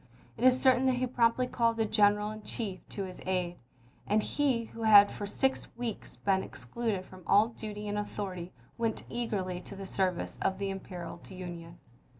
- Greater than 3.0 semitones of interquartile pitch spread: Yes, average, 3.6 semitones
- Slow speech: No, average, 185 wpm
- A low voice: No, high, 210 Hz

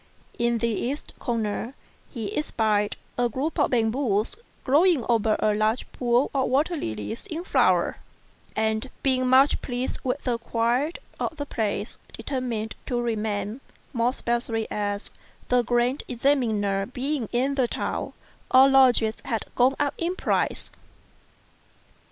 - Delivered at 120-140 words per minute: Yes, slow, 135 wpm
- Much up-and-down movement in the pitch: No, average, 3.4 semitones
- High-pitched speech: Yes, high, 240 Hz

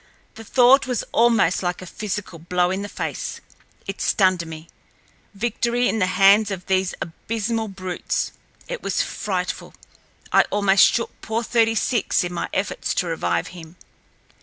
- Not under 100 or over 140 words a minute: No, average, 150 wpm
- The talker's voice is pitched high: Yes, high, 195 Hz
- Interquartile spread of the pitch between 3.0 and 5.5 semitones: Yes, average, 3.9 semitones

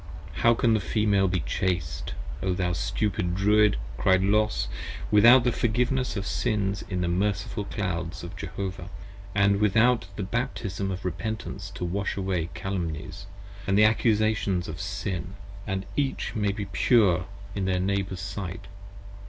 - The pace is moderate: Yes, average, 145 wpm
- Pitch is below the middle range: Yes, low, 100 Hz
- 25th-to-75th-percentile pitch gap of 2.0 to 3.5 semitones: Yes, narrow, 2.6 semitones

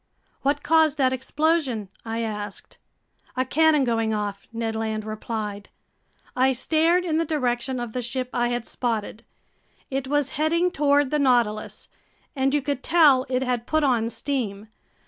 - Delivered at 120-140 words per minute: No, average, 155 wpm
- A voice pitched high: Yes, very high, 255 Hz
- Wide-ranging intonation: No, average, 4.4 semitones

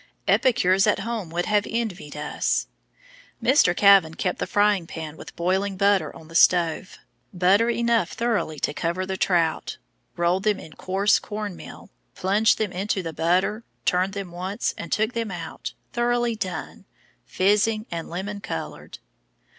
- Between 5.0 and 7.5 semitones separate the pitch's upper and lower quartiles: No, average, 3.3 semitones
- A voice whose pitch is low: No, high, 190 Hz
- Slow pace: No, average, 155 wpm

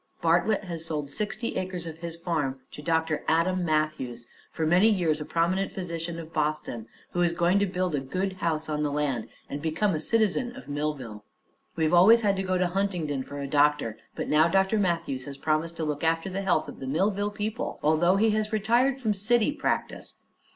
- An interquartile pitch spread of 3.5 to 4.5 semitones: Yes, average, 4.1 semitones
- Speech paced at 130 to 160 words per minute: No, average, 200 wpm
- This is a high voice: No, medium, 170 Hz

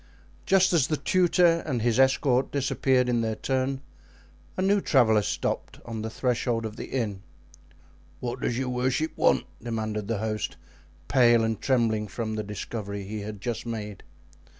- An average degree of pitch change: Yes, average, 3.4 semitones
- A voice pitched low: Yes, low, 120 Hz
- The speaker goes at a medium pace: Yes, average, 160 wpm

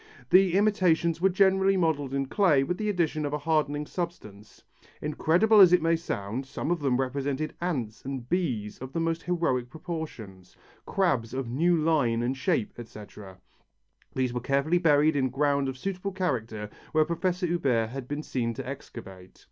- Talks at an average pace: Yes, average, 170 wpm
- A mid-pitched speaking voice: Yes, medium, 145 Hz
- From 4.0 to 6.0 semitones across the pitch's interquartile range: Yes, wide, 5.4 semitones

